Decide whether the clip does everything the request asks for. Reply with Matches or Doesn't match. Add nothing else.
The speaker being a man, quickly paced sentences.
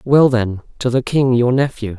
Matches